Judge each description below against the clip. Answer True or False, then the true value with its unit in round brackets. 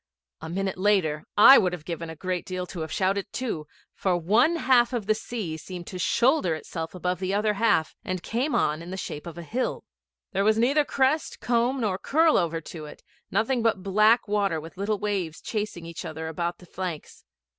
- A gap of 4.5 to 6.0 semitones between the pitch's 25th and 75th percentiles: True (4.9 semitones)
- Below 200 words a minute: False (205 wpm)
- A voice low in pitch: False (190 Hz)